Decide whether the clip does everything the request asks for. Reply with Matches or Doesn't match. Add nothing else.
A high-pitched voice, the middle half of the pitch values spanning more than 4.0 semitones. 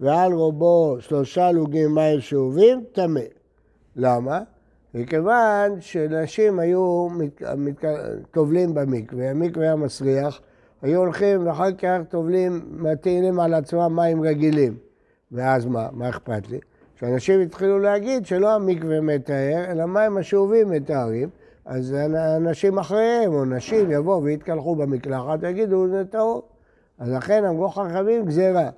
Doesn't match